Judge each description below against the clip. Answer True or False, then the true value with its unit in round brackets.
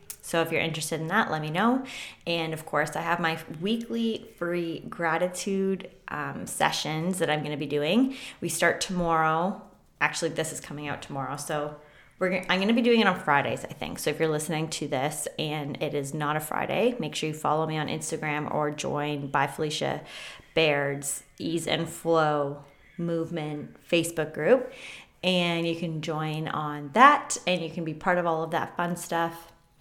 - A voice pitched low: False (160 Hz)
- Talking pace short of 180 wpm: False (190 wpm)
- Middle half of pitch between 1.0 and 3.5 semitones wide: True (2.8 semitones)